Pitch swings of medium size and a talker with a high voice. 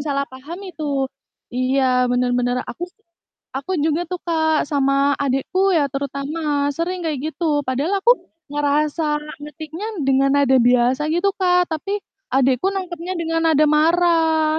Yes: average, 3.6 semitones; very high, 300 Hz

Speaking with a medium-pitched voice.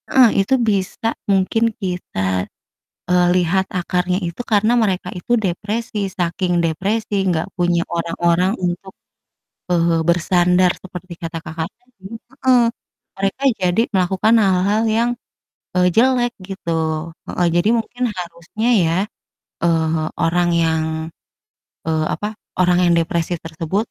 Yes: medium, 180 Hz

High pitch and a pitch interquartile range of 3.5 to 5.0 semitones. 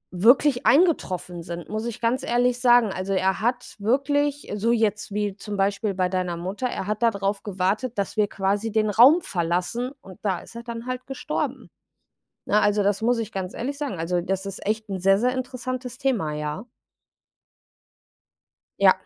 Yes: high, 215 Hz; average, 4.3 semitones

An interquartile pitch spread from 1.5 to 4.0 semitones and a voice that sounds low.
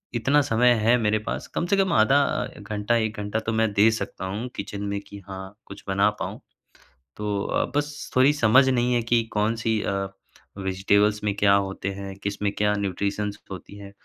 Yes: narrow, 2.5 semitones; low, 105 Hz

